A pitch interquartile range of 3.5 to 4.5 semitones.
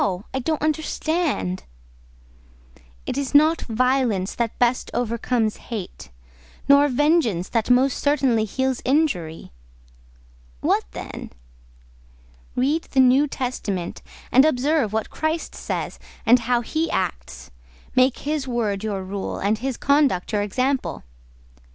No: average, 5.0 semitones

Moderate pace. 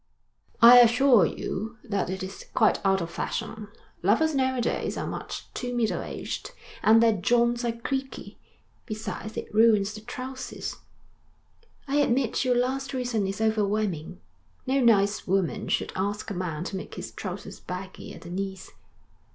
Yes: average, 160 wpm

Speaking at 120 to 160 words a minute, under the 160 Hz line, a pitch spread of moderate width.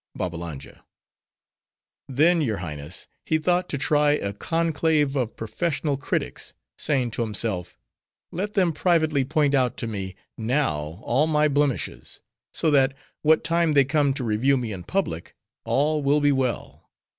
No: average, 145 wpm; medium, 140 Hz; wide, 5.8 semitones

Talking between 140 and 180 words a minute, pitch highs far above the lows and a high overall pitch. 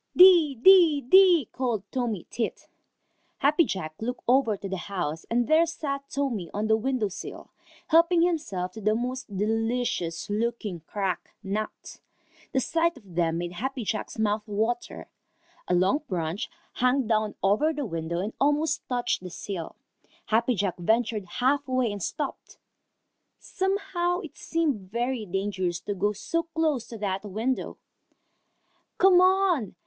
Yes: average, 145 wpm; wide, 6.4 semitones; high, 230 Hz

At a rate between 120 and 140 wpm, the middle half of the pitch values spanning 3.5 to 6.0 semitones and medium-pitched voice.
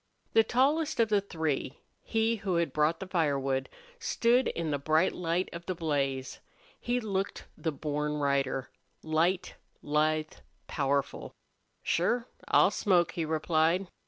Yes: slow, 135 wpm; average, 4.5 semitones; medium, 165 Hz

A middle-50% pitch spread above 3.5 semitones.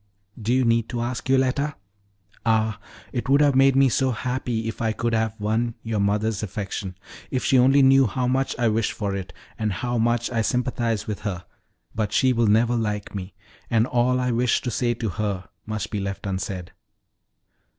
No: average, 3.0 semitones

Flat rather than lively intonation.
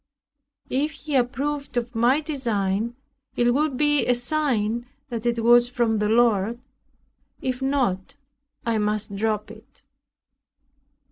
No: average, 3.4 semitones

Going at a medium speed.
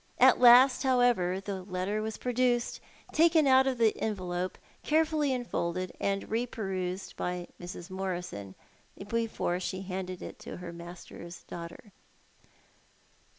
No: slow, 125 wpm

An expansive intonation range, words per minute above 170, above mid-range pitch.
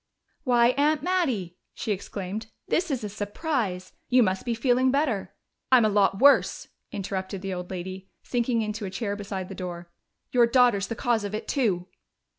No: average, 4.6 semitones; average, 180 wpm; high, 210 Hz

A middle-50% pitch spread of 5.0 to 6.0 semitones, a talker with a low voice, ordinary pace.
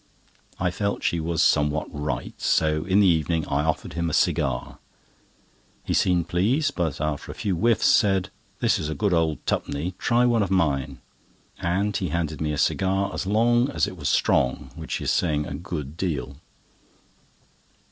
No: average, 4.4 semitones; very low, 85 Hz; average, 170 wpm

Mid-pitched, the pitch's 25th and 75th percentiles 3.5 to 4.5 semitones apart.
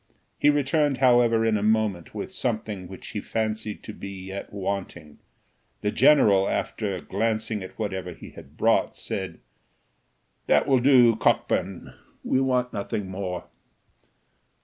No: low, 105 Hz; average, 3.9 semitones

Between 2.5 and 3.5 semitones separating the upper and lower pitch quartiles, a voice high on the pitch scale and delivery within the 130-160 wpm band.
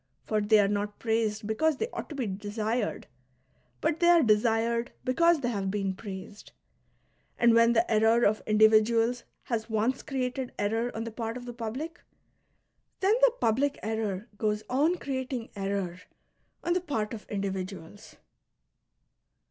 Yes: average, 3.2 semitones; high, 225 Hz; average, 155 wpm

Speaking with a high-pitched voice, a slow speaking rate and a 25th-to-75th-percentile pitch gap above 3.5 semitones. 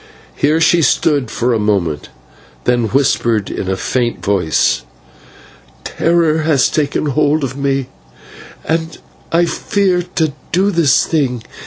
No: medium, 140 Hz; slow, 130 wpm; wide, 5.4 semitones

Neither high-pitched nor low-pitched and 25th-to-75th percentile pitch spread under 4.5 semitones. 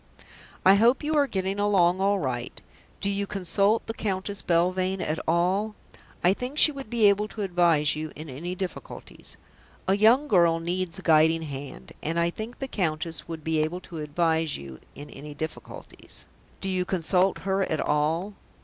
Yes: medium, 180 Hz; average, 3.9 semitones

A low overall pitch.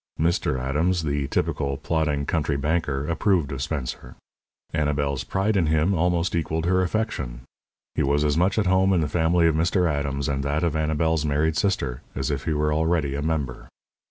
Yes: very low, 80 Hz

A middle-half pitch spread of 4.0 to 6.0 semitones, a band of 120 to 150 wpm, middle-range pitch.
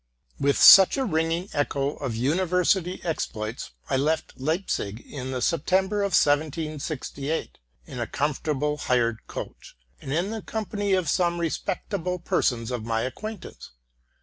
Yes: wide, 5.4 semitones; average, 145 wpm; medium, 155 Hz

